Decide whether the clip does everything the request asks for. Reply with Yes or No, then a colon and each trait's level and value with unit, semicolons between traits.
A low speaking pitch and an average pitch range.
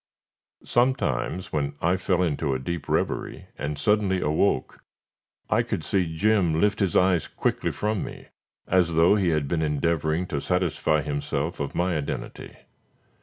Yes: very low, 85 Hz; average, 3.9 semitones